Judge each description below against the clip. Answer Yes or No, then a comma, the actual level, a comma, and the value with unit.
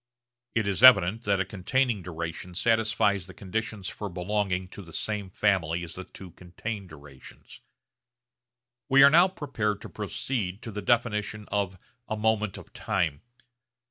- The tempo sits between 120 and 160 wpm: Yes, average, 150 wpm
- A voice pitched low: Yes, low, 100 Hz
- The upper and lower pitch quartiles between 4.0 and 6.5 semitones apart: No, average, 3.4 semitones